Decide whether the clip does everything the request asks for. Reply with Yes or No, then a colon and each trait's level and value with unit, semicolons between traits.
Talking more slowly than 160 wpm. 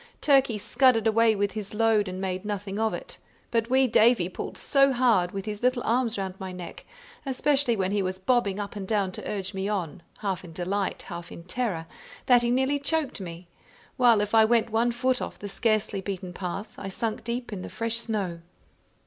No: fast, 205 wpm